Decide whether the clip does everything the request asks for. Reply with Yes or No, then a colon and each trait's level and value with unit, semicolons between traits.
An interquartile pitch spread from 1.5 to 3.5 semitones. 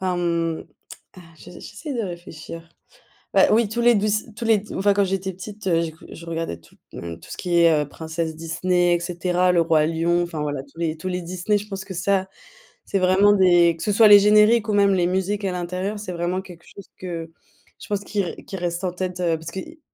Yes: average, 3.0 semitones